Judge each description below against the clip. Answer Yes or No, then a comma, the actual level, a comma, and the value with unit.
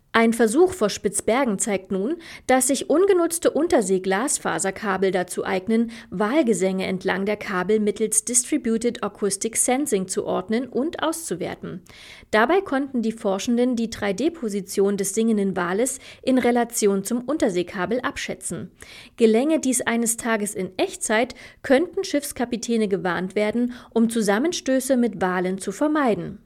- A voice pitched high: Yes, high, 225 Hz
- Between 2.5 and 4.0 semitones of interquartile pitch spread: No, average, 4.6 semitones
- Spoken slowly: Yes, slow, 120 wpm